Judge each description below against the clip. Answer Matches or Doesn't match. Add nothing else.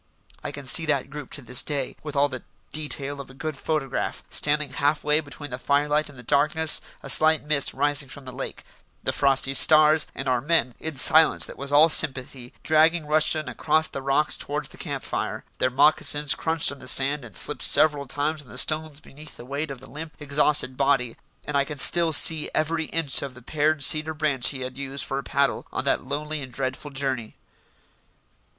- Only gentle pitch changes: Matches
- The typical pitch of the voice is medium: Matches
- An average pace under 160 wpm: Doesn't match